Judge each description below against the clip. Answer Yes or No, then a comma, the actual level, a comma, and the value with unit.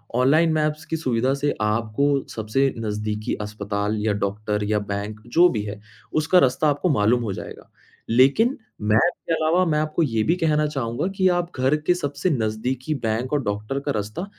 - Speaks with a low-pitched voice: Yes, low, 130 Hz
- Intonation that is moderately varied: No, wide, 6.2 semitones